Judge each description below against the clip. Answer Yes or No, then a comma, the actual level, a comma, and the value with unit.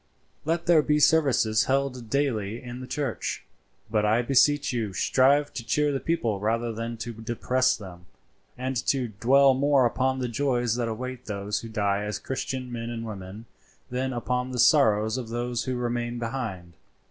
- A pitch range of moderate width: Yes, average, 3.1 semitones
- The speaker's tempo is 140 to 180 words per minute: Yes, average, 170 wpm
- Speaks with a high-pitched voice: No, low, 120 Hz